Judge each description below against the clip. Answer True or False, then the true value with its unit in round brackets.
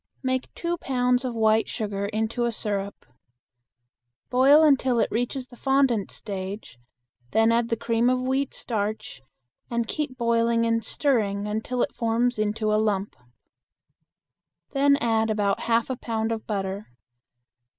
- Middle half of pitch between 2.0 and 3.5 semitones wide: True (2.8 semitones)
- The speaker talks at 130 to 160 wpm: True (140 wpm)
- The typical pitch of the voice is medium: False (230 Hz)